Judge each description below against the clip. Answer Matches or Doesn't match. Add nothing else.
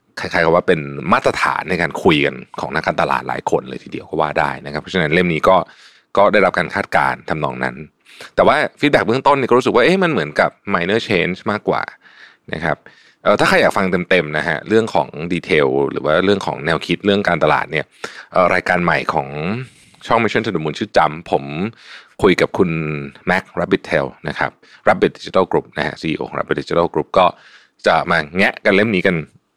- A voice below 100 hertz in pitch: Matches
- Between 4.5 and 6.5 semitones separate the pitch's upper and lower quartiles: Doesn't match